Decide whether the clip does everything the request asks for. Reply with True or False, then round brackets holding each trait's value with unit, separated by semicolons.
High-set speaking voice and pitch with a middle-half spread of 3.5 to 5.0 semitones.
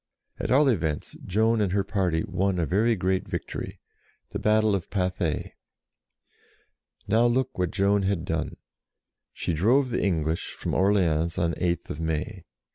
False (95 Hz; 4.1 semitones)